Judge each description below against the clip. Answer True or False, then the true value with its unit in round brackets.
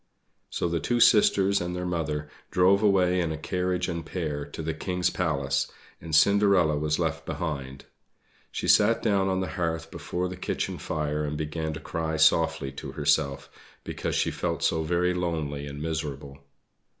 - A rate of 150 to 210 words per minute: True (170 wpm)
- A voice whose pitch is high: False (80 Hz)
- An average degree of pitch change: True (3.2 semitones)